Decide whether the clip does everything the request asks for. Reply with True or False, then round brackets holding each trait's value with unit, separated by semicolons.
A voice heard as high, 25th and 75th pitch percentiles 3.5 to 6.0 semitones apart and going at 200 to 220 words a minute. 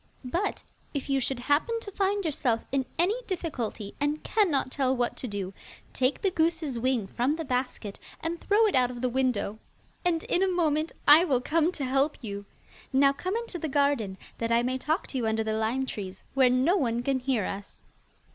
True (270 Hz; 5.2 semitones; 205 wpm)